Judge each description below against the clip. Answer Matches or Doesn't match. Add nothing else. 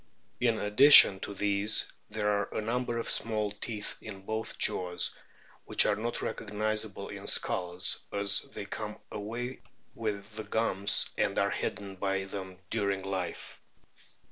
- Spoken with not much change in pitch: Matches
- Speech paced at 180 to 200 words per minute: Doesn't match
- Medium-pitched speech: Doesn't match